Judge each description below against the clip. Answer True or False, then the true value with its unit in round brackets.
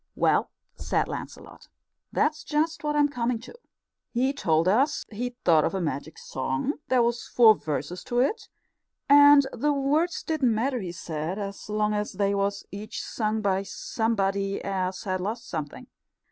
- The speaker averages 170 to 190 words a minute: False (160 wpm)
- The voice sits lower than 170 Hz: False (215 Hz)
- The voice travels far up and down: True (5.8 semitones)